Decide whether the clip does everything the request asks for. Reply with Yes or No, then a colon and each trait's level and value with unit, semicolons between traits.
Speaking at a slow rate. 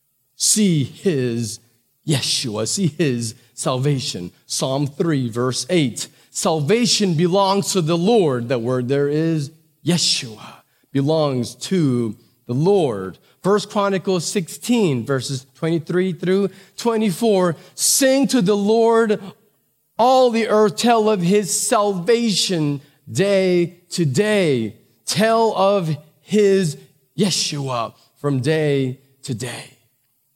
Yes: slow, 105 wpm